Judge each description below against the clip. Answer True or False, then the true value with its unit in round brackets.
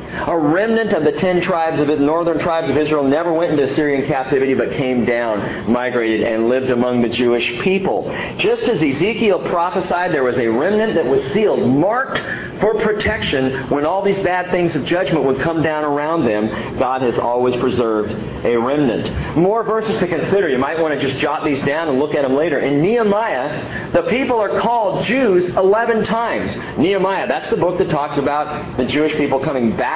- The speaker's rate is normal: True (195 wpm)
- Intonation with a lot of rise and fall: True (6.3 semitones)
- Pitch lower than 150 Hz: False (155 Hz)